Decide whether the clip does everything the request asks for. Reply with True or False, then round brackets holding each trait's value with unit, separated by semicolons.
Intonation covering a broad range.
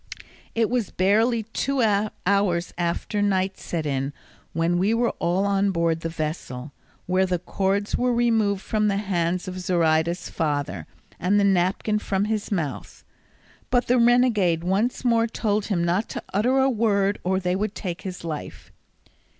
False (3.8 semitones)